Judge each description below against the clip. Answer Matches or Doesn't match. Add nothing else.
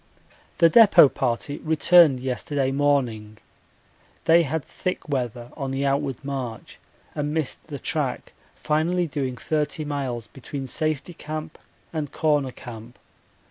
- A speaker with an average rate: Doesn't match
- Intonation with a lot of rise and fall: Doesn't match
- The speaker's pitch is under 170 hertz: Matches